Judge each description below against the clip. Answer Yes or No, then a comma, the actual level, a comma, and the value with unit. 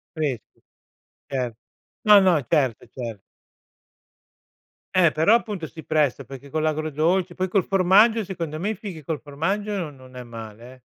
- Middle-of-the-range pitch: Yes, medium, 155 Hz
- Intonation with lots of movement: Yes, wide, 5.9 semitones